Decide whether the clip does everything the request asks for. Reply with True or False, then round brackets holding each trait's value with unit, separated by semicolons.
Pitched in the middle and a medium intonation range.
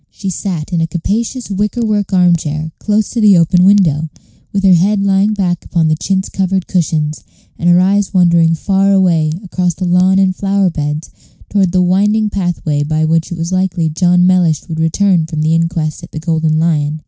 True (180 Hz; 3.1 semitones)